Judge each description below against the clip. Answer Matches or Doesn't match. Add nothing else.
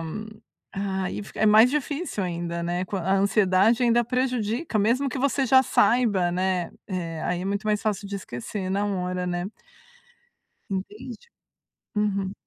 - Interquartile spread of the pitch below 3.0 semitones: Doesn't match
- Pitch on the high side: Matches